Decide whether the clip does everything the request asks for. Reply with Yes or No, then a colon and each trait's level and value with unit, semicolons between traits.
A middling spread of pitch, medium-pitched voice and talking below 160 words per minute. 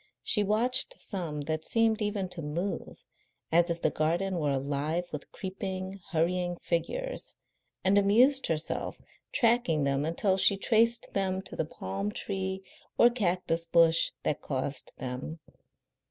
Yes: average, 4.3 semitones; medium, 180 Hz; average, 140 wpm